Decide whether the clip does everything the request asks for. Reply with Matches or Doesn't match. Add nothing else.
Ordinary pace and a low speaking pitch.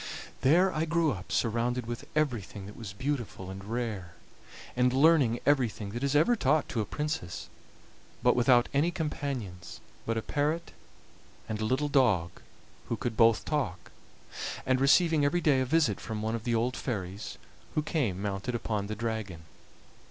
Matches